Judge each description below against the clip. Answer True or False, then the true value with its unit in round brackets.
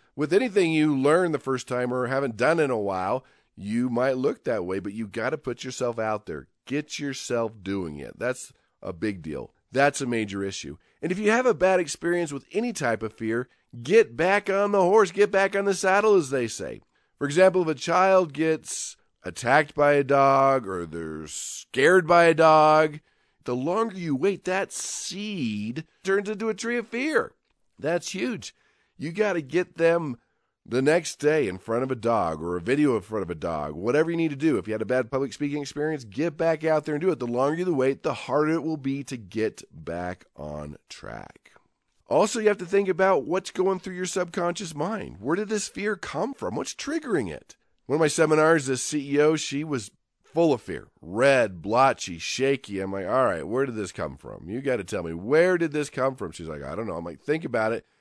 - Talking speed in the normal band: False (220 wpm)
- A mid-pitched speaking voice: True (150 Hz)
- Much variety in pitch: True (6.8 semitones)